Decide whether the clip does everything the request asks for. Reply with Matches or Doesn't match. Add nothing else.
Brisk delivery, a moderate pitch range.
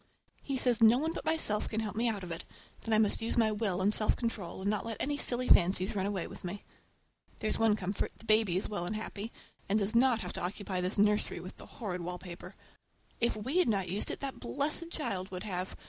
Matches